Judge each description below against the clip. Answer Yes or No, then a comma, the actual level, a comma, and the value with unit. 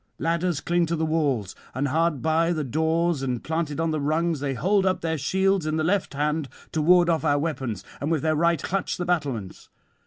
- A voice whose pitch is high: No, medium, 160 Hz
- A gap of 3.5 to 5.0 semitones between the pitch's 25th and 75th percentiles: No, average, 2.8 semitones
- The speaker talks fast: Yes, fast, 215 wpm